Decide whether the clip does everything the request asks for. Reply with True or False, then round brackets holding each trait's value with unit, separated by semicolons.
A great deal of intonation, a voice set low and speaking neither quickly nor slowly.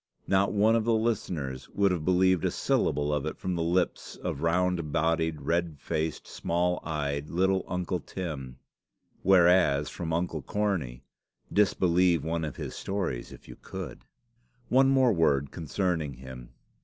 False (3.8 semitones; 85 Hz; 150 wpm)